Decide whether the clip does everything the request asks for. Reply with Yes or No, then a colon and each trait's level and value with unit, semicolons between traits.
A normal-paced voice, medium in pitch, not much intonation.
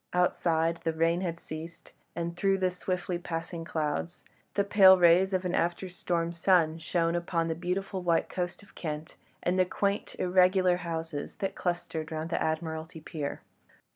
Yes: average, 165 wpm; medium, 170 Hz; narrow, 1.9 semitones